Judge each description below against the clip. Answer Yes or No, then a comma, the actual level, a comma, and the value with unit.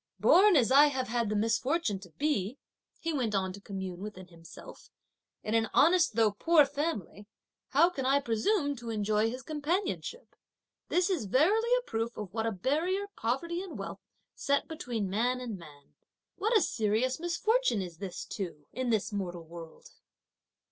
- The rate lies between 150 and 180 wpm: Yes, average, 170 wpm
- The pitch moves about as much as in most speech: No, wide, 7.4 semitones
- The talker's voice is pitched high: Yes, high, 240 Hz